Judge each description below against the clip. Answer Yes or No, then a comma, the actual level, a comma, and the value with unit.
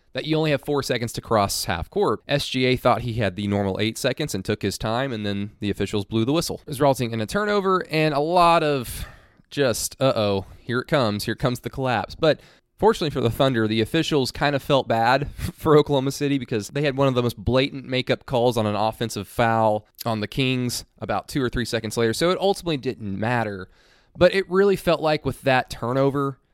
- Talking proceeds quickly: Yes, fast, 225 wpm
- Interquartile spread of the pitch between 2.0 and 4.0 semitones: No, average, 4.6 semitones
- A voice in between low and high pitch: No, low, 125 Hz